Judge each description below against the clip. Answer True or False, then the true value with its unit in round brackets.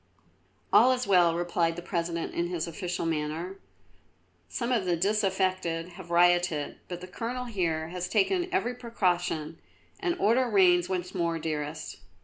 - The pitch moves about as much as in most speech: True (3.1 semitones)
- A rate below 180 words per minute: True (145 wpm)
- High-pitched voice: False (175 Hz)